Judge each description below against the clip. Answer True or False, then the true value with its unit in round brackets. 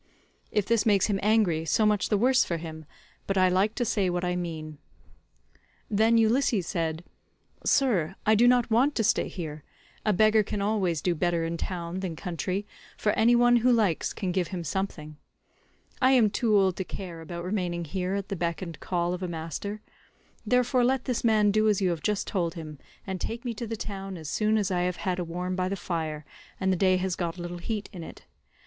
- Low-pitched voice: False (190 Hz)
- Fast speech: True (220 wpm)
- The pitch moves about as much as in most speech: True (3.9 semitones)